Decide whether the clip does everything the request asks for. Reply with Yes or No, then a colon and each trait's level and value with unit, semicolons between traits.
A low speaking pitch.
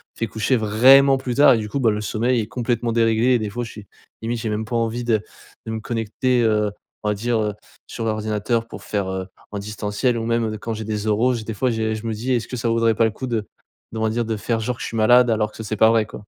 Yes: low, 115 Hz